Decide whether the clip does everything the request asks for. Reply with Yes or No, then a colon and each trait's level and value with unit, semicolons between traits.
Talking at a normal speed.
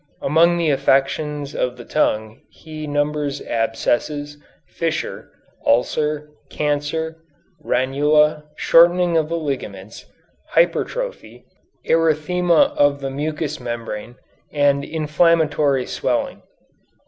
No: slow, 90 wpm